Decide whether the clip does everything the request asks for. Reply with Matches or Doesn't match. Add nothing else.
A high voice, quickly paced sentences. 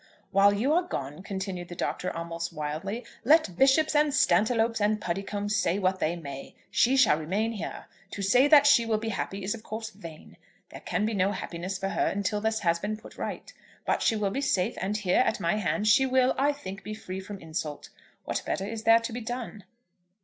Matches